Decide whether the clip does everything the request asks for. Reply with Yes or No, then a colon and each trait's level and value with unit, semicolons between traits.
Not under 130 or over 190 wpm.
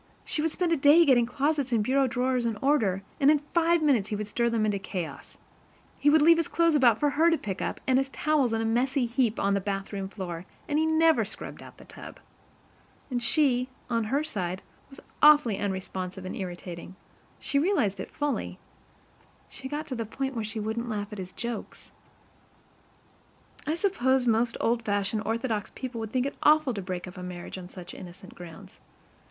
No: average, 200 wpm